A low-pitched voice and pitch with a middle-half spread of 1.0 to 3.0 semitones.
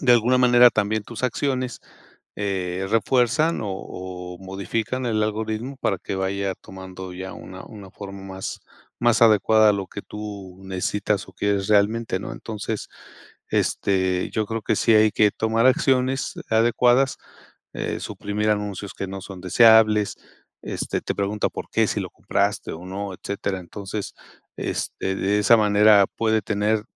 Yes: low, 105 Hz; narrow, 2.5 semitones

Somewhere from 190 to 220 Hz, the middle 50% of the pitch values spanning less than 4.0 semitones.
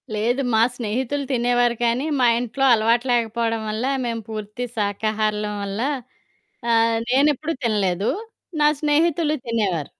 No: high, 230 Hz; average, 2.8 semitones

